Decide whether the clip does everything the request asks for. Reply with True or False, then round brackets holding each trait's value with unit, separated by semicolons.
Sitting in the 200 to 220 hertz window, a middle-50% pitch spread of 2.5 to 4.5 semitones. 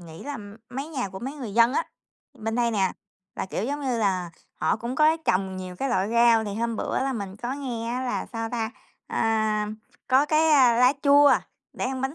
False (235 Hz; 4.1 semitones)